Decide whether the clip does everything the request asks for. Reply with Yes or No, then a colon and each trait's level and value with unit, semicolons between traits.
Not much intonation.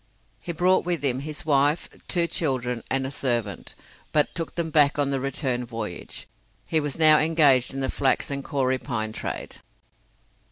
No: average, 3.2 semitones